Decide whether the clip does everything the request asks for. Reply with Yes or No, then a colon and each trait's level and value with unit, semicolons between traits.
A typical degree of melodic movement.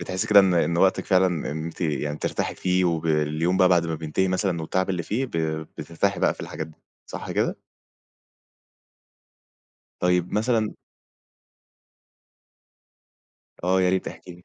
No: narrow, 2.2 semitones